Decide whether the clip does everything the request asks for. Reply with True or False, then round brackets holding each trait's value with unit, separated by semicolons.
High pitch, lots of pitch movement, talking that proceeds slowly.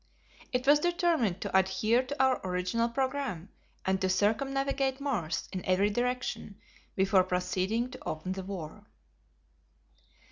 True (215 Hz; 6.0 semitones; 130 wpm)